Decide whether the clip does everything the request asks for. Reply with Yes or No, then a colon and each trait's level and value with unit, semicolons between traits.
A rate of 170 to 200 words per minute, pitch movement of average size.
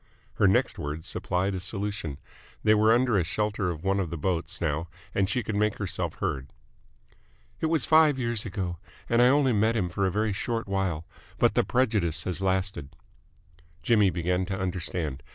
Yes: average, 180 wpm; average, 3.8 semitones